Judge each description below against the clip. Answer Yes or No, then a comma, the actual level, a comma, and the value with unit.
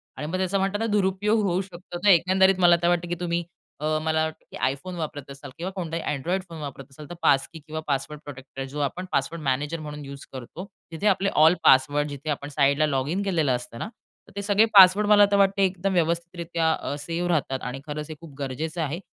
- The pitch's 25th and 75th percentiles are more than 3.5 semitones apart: Yes, average, 4.3 semitones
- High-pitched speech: No, medium, 165 Hz